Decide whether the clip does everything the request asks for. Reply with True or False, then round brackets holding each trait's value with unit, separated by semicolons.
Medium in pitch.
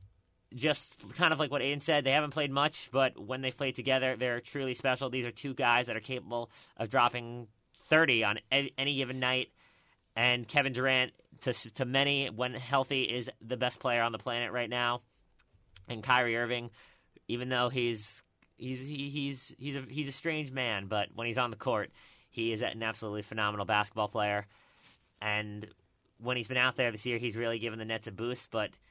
False (125 Hz)